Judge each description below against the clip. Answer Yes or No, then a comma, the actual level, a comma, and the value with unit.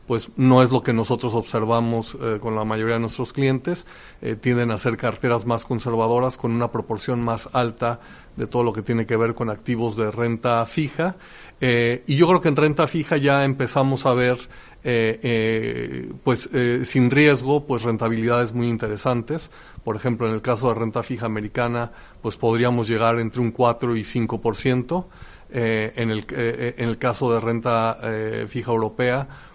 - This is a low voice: Yes, low, 120 Hz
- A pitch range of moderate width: No, narrow, 1.9 semitones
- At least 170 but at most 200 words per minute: Yes, average, 180 wpm